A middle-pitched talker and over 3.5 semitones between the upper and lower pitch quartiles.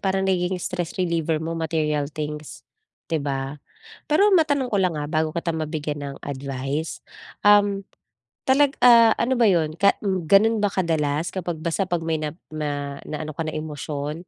Yes: medium, 165 Hz; average, 4.4 semitones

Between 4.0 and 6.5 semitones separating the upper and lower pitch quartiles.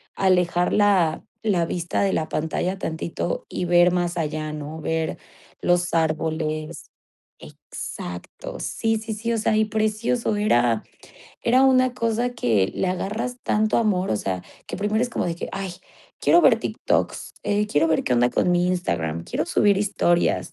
Yes: average, 5.2 semitones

